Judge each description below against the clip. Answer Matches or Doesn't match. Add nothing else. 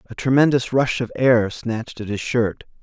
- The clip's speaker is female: Doesn't match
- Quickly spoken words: Doesn't match